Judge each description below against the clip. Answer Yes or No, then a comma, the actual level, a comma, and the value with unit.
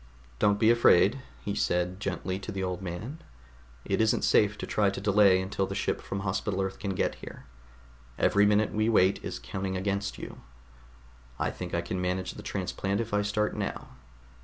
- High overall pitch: No, low, 100 Hz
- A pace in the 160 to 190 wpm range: Yes, average, 185 wpm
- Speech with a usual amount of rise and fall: No, narrow, 1.9 semitones